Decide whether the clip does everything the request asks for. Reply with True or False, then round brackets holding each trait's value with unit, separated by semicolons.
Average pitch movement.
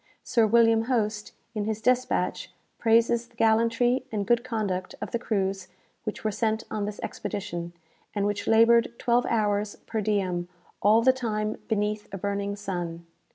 False (2.2 semitones)